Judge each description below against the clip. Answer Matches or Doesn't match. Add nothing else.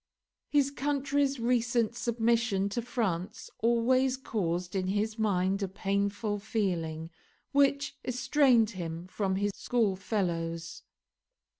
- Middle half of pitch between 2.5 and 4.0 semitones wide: Doesn't match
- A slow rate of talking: Matches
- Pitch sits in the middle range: Doesn't match